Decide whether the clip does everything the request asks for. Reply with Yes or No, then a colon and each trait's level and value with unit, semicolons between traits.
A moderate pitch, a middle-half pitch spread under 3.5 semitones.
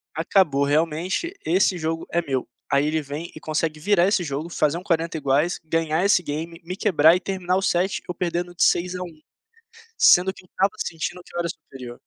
Yes: medium, 165 Hz; average, 2.7 semitones